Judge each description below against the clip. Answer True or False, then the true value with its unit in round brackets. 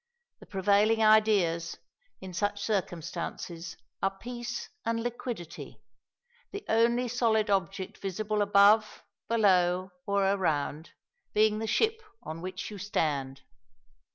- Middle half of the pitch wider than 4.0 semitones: False (3.6 semitones)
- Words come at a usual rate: False (110 wpm)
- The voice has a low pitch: False (200 Hz)